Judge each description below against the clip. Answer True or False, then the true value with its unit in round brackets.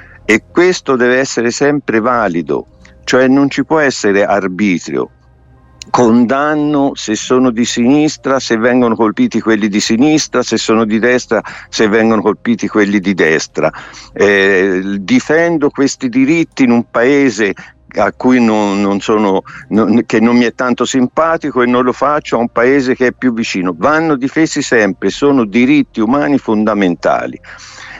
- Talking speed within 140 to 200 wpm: True (150 wpm)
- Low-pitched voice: True (120 Hz)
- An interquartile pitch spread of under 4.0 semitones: False (4.6 semitones)